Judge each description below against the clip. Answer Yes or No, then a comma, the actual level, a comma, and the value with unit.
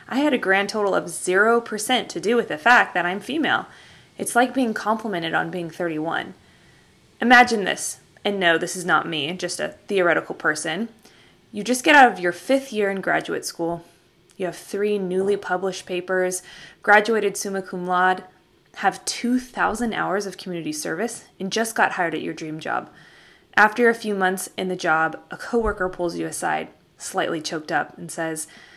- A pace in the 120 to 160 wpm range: No, average, 180 wpm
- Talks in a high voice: Yes, high, 195 Hz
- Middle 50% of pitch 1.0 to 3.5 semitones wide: No, average, 4.4 semitones